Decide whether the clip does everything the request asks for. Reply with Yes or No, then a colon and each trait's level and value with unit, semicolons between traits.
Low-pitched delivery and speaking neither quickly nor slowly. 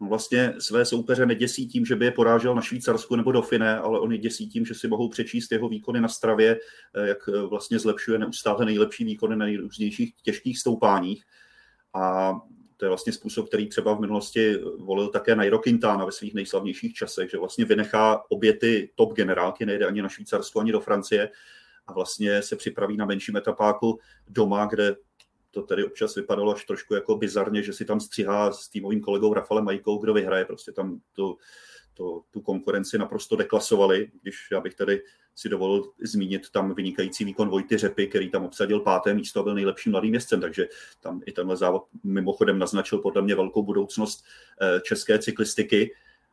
No: low, 115 Hz; fast, 180 wpm